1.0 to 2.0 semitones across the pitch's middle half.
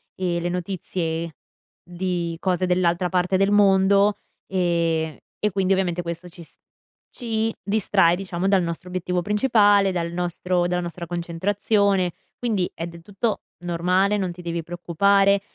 No: narrow, 2.4 semitones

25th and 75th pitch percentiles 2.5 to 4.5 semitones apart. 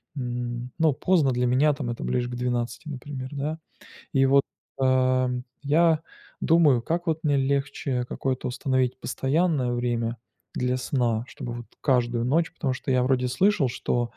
Yes: average, 2.8 semitones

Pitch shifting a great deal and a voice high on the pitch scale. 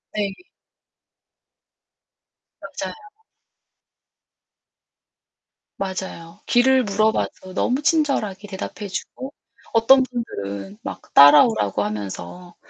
Yes: wide, 6.7 semitones; high, 200 Hz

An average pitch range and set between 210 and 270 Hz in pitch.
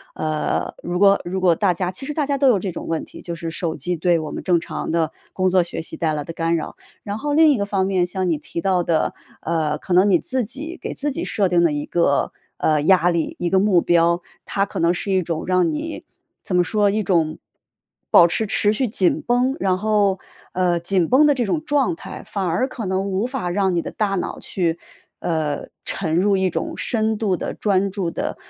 No: average, 3.6 semitones; medium, 185 Hz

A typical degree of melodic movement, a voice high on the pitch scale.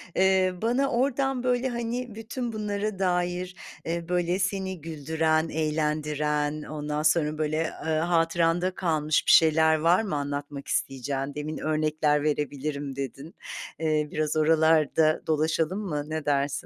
No: average, 3.6 semitones; medium, 160 Hz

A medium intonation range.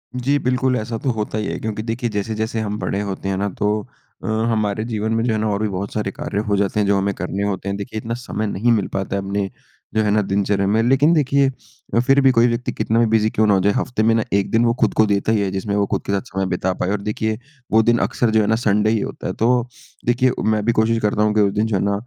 No: narrow, 2.2 semitones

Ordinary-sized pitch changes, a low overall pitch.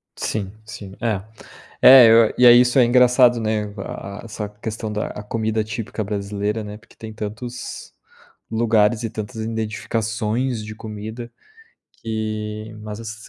No: narrow, 1.5 semitones; low, 110 Hz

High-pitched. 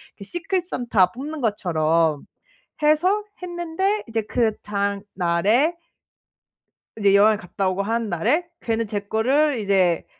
Yes: high, 220 Hz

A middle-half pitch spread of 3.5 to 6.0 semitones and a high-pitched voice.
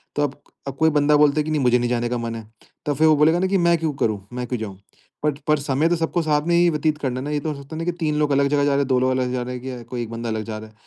No: average, 3.8 semitones; medium, 140 Hz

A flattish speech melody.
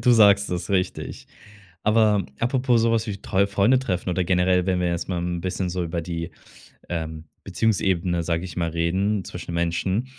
No: average, 3.1 semitones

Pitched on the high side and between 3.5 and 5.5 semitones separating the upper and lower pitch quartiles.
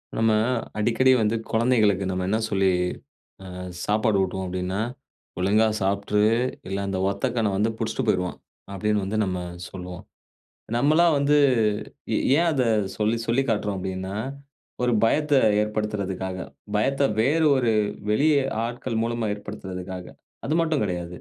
No: low, 105 Hz; average, 3.8 semitones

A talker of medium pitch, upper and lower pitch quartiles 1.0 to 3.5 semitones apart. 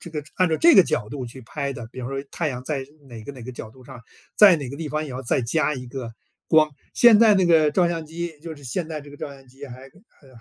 No: medium, 145 Hz; average, 4.1 semitones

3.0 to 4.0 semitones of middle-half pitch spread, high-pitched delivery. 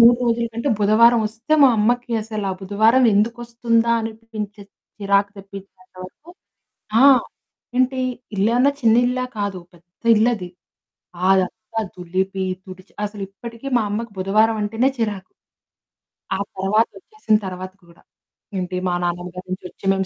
Yes: average, 3.3 semitones; high, 210 Hz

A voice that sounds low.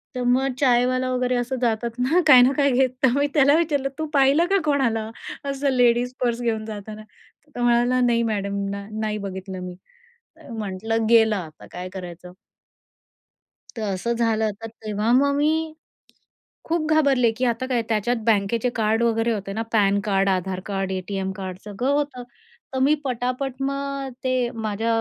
No: high, 235 Hz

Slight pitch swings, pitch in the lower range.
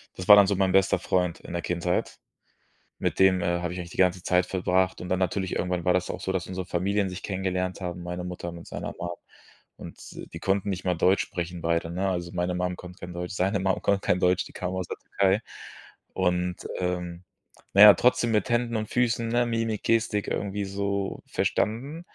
Yes: narrow, 2.0 semitones; very low, 95 Hz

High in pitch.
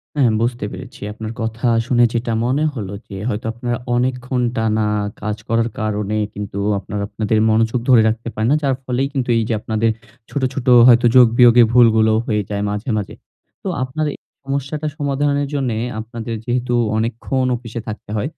No: low, 120 Hz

